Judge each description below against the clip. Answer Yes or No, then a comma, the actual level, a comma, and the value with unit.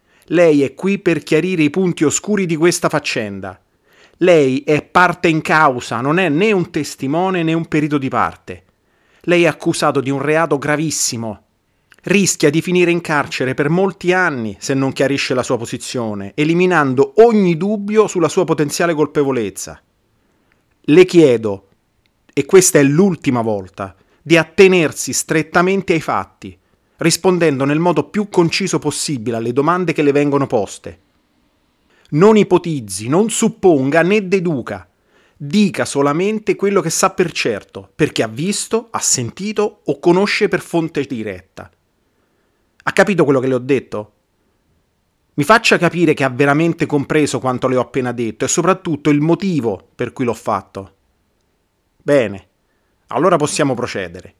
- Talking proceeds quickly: No, average, 145 wpm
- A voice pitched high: No, medium, 150 Hz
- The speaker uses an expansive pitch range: Yes, wide, 6.2 semitones